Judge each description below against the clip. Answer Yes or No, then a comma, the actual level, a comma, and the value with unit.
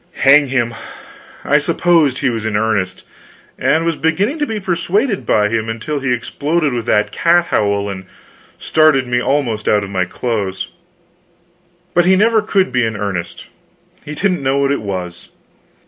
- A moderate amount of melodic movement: No, wide, 7.9 semitones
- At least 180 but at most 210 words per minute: No, average, 165 wpm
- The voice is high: No, low, 135 Hz